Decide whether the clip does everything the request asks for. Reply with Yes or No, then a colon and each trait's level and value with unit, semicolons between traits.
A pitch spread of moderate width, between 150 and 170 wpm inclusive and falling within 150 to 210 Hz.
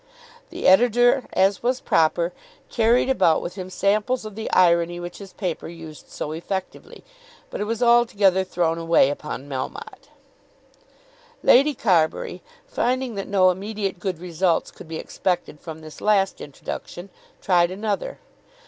No: average, 4.5 semitones; average, 140 wpm; high, 190 Hz